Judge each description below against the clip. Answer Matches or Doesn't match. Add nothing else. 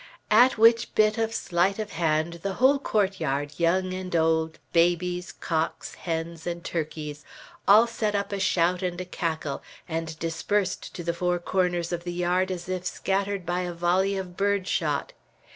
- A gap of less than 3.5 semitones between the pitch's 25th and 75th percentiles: Matches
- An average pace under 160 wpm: Doesn't match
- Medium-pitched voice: Matches